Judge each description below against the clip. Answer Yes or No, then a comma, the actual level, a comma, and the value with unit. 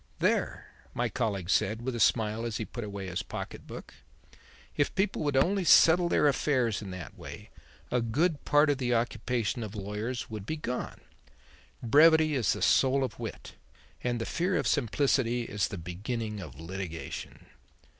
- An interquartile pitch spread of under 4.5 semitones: No, average, 5.0 semitones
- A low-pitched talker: Yes, low, 120 Hz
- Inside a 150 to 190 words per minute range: Yes, average, 170 wpm